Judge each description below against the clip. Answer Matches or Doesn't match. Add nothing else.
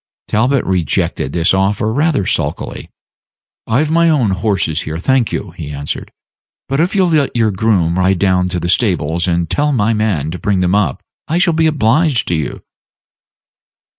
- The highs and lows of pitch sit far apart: Matches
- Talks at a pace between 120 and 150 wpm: Doesn't match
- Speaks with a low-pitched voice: Matches